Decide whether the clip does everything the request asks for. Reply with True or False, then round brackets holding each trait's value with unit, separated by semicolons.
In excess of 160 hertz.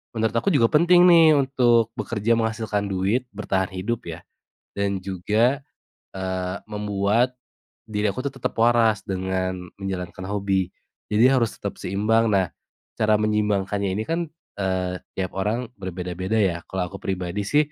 False (105 Hz)